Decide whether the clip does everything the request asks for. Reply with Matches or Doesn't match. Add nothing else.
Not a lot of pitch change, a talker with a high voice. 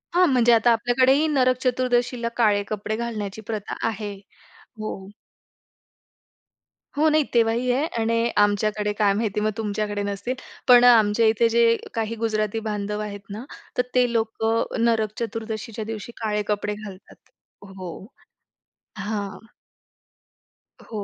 Matches